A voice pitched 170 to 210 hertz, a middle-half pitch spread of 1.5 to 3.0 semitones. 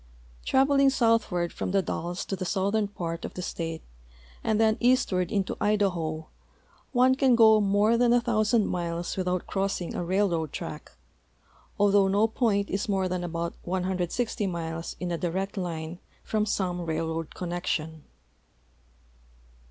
No: high, 190 Hz; average, 3.8 semitones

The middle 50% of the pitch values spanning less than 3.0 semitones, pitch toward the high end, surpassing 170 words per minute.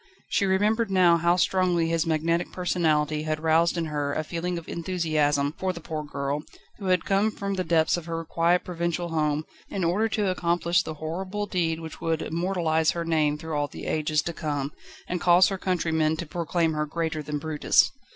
No: narrow, 2.4 semitones; medium, 165 Hz; average, 195 wpm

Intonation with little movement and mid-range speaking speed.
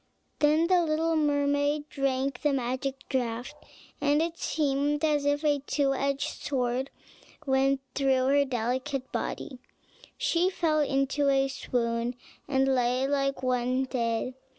No: narrow, 2.1 semitones; slow, 130 wpm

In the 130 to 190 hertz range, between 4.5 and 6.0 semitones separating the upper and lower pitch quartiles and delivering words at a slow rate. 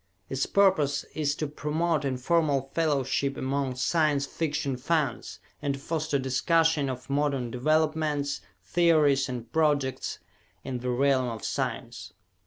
No: medium, 140 Hz; average, 2.9 semitones; slow, 125 wpm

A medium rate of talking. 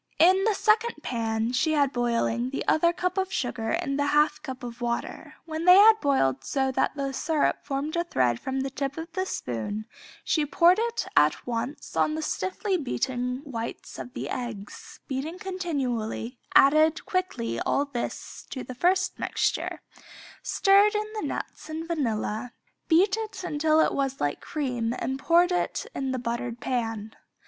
Yes: average, 165 wpm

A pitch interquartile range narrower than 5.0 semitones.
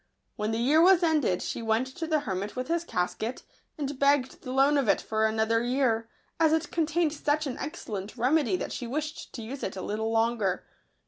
No: wide, 5.4 semitones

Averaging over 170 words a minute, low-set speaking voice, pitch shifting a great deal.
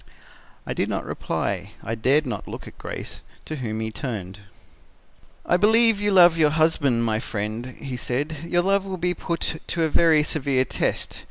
No: average, 180 wpm; medium, 150 Hz; wide, 6.8 semitones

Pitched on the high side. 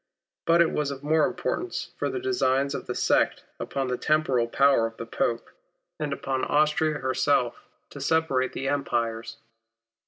No: medium, 140 Hz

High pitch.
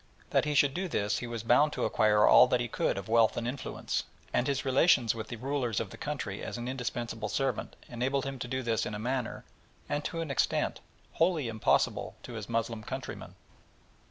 No: low, 120 Hz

